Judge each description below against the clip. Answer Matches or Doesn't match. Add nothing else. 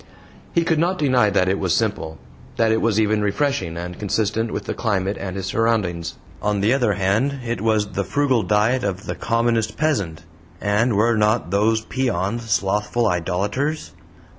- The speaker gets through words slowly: Doesn't match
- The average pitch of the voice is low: Matches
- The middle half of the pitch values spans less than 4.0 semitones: Matches